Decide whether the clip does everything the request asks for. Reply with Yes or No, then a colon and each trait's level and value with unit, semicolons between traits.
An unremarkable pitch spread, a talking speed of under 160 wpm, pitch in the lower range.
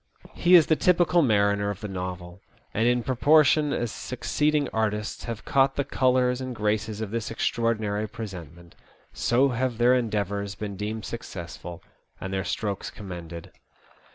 Yes: average, 4.0 semitones; average, 150 wpm; low, 110 Hz